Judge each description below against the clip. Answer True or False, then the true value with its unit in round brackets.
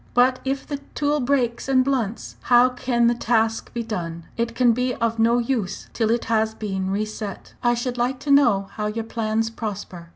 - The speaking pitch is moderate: False (235 Hz)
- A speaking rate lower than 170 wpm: False (200 wpm)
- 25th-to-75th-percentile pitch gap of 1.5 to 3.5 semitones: True (2.5 semitones)